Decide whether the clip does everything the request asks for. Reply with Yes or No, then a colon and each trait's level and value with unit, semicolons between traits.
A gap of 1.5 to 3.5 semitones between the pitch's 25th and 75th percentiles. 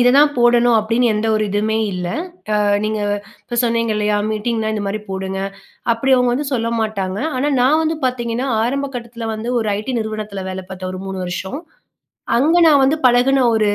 Yes: average, 3.0 semitones